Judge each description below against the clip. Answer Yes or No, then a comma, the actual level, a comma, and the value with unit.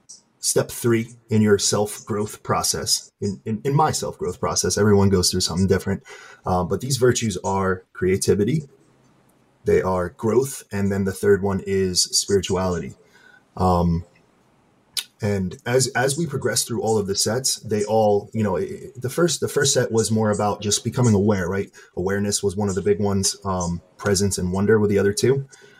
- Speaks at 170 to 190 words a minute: Yes, average, 180 wpm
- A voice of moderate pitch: No, low, 100 Hz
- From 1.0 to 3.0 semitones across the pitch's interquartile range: Yes, narrow, 2.6 semitones